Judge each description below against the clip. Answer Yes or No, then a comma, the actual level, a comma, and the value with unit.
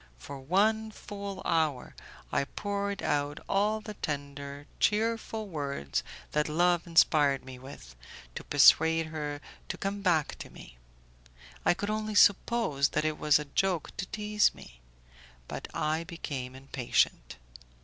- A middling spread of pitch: No, wide, 6.2 semitones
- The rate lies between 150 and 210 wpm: No, average, 140 wpm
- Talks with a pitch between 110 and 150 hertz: No, medium, 160 Hz